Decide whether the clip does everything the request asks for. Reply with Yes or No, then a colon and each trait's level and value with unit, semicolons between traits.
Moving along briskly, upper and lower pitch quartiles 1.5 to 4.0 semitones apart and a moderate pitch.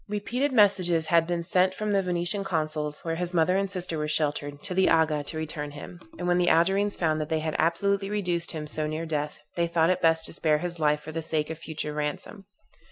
Yes: fast, 230 wpm; average, 2.9 semitones; medium, 165 Hz